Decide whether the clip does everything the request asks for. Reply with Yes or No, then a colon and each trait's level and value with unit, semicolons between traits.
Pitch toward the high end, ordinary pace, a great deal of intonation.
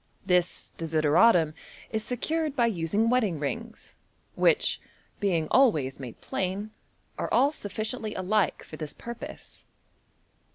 No: high, 205 Hz; slow, 120 wpm; wide, 6.0 semitones